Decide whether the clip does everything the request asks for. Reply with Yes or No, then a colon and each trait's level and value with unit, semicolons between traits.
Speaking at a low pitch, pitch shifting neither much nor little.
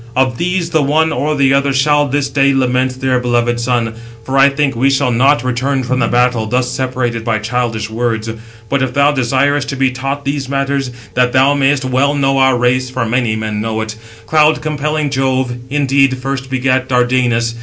No: low, 130 Hz; narrow, 2.2 semitones